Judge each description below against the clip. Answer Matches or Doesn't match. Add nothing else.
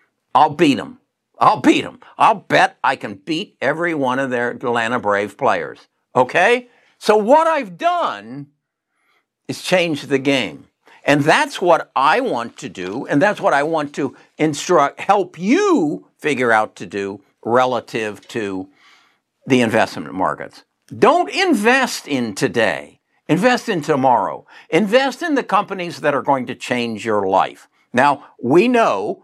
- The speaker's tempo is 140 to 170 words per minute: Matches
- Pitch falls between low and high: Matches